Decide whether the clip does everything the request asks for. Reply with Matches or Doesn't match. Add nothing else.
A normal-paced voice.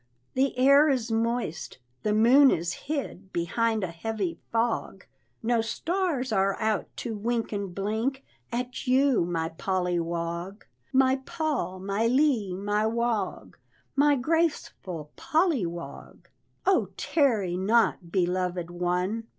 Doesn't match